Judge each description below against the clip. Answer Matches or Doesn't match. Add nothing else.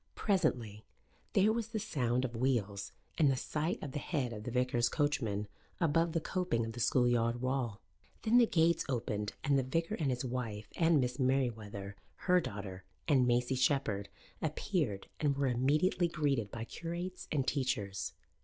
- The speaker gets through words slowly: Doesn't match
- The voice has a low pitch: Matches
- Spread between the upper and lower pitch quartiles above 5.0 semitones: Matches